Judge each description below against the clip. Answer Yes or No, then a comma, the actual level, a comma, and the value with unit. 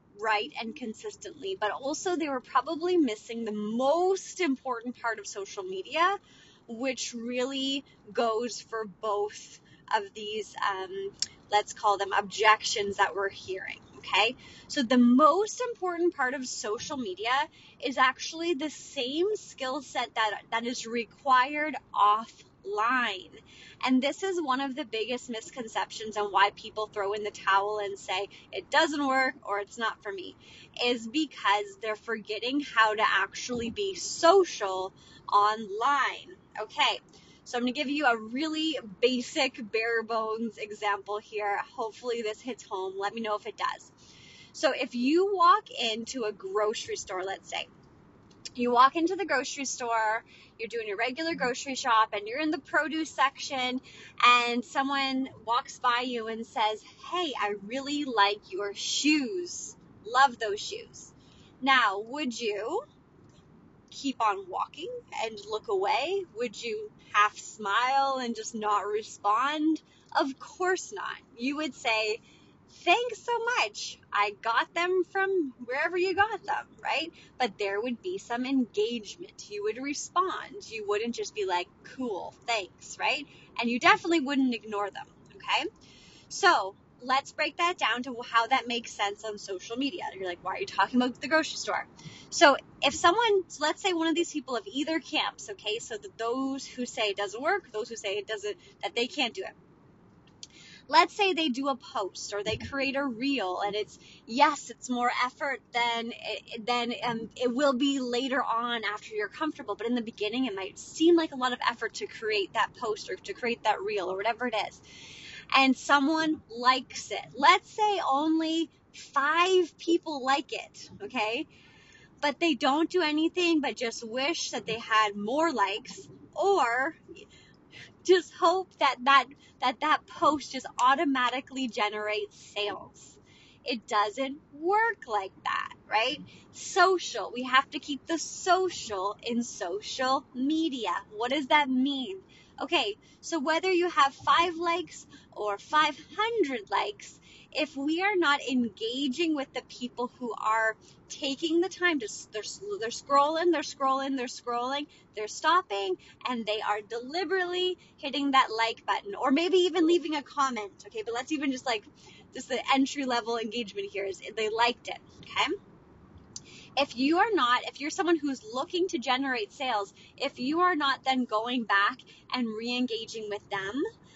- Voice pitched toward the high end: Yes, very high, 255 Hz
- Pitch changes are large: Yes, wide, 6.2 semitones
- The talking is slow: No, average, 160 wpm